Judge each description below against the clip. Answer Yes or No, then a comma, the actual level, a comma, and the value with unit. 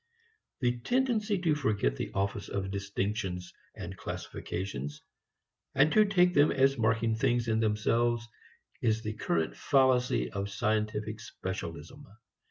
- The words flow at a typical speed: No, slow, 125 wpm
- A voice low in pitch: Yes, low, 110 Hz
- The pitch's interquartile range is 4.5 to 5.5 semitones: Yes, average, 5.1 semitones